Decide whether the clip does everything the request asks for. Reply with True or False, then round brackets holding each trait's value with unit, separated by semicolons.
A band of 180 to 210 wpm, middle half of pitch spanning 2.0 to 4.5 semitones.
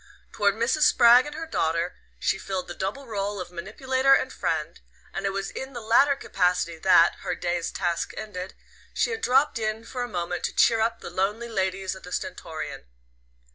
False (190 wpm; 5.2 semitones)